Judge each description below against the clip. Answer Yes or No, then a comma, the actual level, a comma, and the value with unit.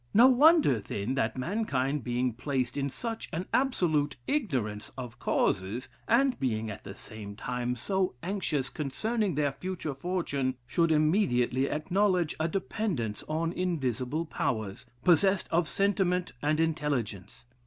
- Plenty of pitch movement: Yes, wide, 6.8 semitones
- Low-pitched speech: No, medium, 150 Hz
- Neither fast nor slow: No, slow, 130 wpm